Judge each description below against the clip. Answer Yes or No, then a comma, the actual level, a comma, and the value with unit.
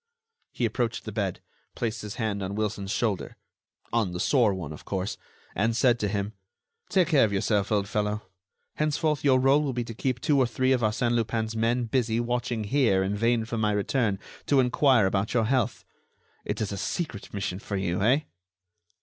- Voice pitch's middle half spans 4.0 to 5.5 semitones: No, average, 3.4 semitones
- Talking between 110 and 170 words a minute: No, average, 185 wpm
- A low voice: Yes, low, 115 Hz